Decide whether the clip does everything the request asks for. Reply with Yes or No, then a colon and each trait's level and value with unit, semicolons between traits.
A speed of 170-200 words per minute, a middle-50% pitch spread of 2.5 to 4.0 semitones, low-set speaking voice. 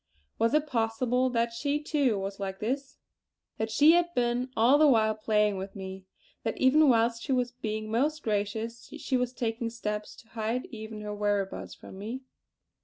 No: average, 180 wpm; average, 3.3 semitones; high, 230 Hz